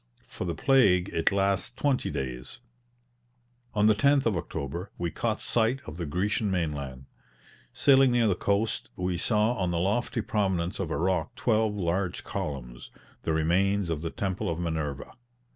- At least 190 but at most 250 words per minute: No, average, 160 wpm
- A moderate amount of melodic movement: Yes, average, 4.6 semitones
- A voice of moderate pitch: No, very low, 95 Hz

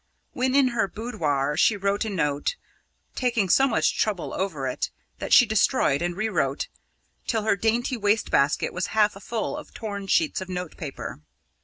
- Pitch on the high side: Yes, high, 205 Hz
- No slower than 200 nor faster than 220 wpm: No, average, 165 wpm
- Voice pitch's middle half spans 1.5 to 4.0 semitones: No, average, 4.8 semitones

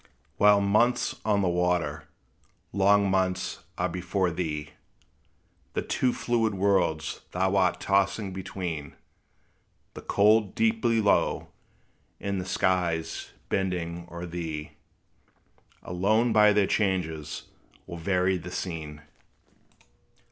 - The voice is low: Yes, very low, 95 Hz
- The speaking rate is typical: No, slow, 105 wpm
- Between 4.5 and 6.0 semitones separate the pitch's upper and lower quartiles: No, average, 2.8 semitones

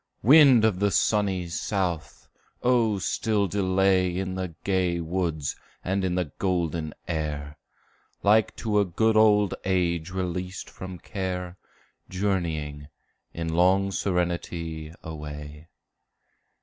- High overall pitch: No, very low, 90 Hz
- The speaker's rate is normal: No, slow, 110 wpm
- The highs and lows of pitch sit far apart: No, average, 2.9 semitones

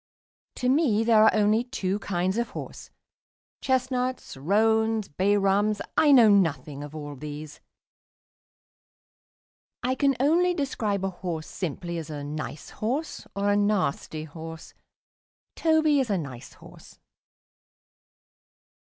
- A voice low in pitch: No, high, 205 Hz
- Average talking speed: No, slow, 125 wpm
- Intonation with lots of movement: Yes, wide, 7.5 semitones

